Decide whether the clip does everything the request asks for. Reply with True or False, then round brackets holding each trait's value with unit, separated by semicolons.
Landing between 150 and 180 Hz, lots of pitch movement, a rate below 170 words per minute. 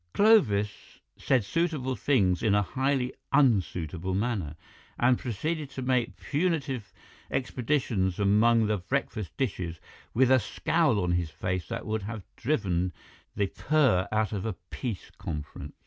False (110 Hz; 5.9 semitones; 135 wpm)